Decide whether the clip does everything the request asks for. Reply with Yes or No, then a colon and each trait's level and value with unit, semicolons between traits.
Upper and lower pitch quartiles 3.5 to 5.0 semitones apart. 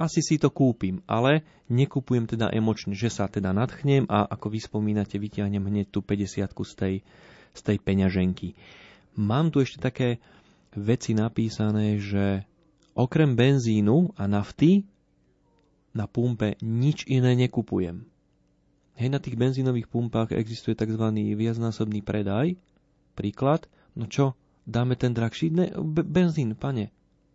Yes: average, 4.7 semitones